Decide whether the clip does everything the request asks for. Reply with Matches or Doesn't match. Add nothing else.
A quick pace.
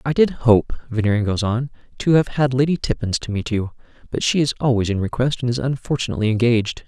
Matches